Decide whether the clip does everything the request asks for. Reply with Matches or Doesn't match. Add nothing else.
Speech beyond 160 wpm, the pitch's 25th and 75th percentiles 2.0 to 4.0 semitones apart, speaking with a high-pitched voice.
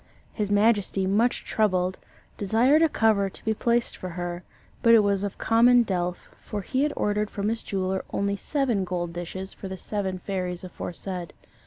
Matches